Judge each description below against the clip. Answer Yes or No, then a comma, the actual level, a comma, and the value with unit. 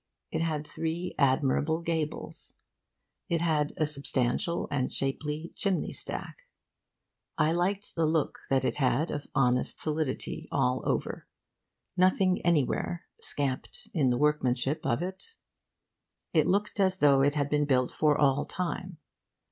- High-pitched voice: No, medium, 150 Hz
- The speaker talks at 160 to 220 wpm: No, slow, 135 wpm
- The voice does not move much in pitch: No, average, 3.8 semitones